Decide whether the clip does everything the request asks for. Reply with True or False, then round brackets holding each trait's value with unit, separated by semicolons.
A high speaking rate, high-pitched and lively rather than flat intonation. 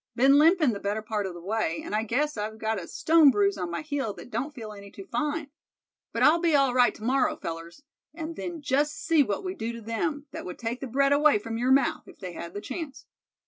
True (250 wpm; 245 Hz; 6.0 semitones)